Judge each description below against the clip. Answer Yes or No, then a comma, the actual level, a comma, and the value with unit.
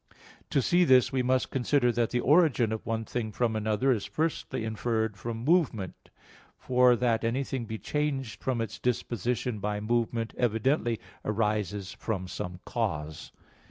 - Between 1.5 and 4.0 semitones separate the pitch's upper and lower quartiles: Yes, average, 2.7 semitones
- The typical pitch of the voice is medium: No, low, 115 Hz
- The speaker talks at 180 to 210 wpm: No, average, 150 wpm